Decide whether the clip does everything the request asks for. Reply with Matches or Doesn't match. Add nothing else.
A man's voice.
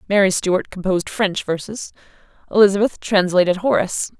Doesn't match